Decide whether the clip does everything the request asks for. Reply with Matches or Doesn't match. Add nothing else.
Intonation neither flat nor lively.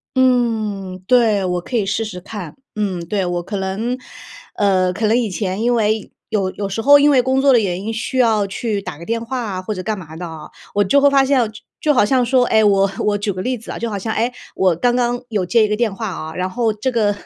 Matches